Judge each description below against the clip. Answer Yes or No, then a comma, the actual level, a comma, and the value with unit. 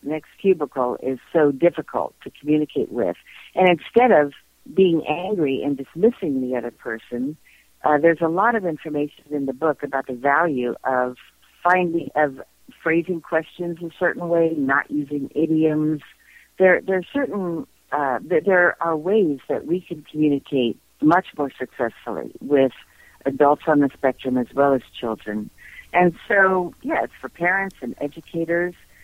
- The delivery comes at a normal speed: Yes, average, 155 wpm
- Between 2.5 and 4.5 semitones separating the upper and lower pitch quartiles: Yes, average, 4.2 semitones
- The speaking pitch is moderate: Yes, medium, 155 Hz